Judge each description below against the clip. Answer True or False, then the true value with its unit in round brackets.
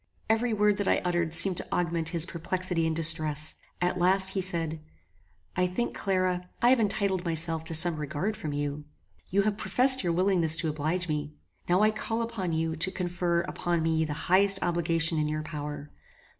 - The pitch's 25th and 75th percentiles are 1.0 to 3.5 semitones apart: True (3.0 semitones)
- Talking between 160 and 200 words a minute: True (185 wpm)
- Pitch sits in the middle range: True (175 Hz)